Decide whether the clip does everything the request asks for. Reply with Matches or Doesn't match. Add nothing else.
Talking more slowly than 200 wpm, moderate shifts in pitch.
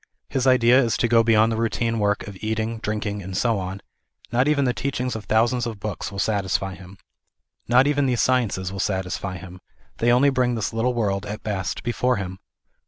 Doesn't match